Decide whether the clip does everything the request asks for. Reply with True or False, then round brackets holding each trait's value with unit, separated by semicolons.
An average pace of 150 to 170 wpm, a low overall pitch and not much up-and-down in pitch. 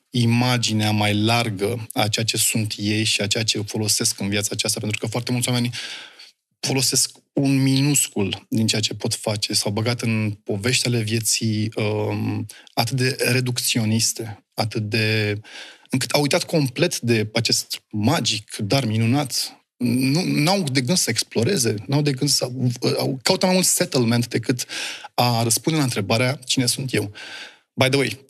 False (160 wpm; 120 Hz; 3.3 semitones)